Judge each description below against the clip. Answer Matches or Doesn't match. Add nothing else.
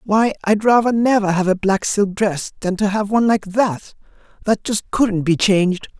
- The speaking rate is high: Doesn't match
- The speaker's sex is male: Matches